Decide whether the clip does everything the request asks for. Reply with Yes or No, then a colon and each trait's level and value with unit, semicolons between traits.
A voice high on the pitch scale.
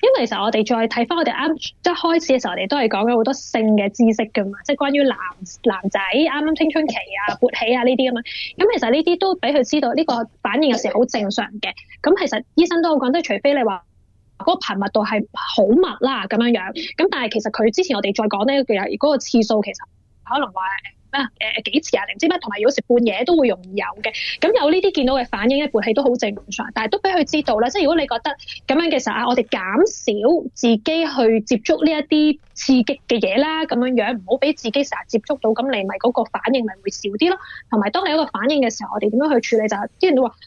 Yes: very high, 250 Hz